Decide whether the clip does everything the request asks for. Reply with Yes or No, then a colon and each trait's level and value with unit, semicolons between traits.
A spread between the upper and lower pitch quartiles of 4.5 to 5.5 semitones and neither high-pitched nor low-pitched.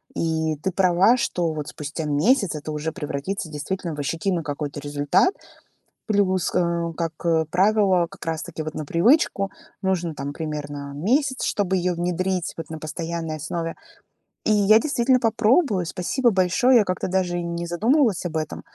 No: average, 4.0 semitones; medium, 175 Hz